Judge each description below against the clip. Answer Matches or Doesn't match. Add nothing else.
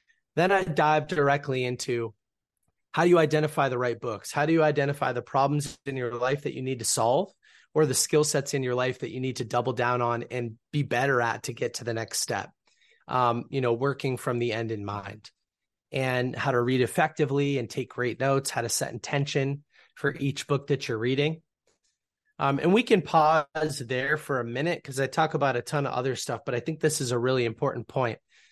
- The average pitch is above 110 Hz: Matches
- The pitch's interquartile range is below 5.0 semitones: Matches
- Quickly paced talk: Matches